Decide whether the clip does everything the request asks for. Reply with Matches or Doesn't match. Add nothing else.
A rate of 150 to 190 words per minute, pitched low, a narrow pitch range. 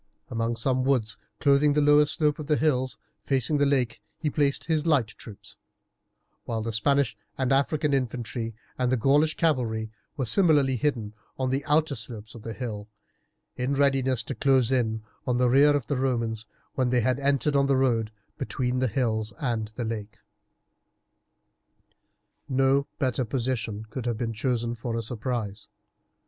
Doesn't match